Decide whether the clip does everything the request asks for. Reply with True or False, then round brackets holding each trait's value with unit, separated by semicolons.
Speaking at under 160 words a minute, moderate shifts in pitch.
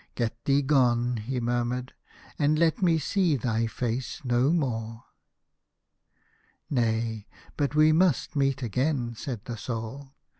True (135 wpm; 3.6 semitones)